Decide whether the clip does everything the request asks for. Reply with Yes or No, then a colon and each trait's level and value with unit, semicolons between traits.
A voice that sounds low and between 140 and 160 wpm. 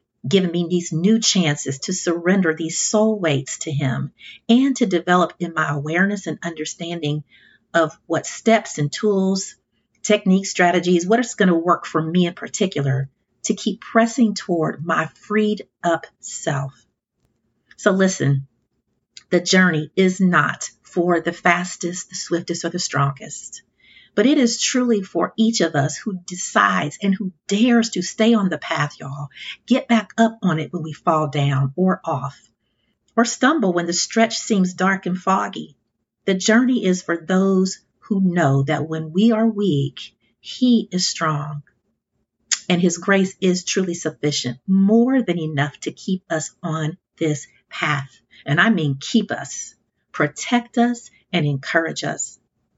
No: medium, 180 Hz; average, 155 wpm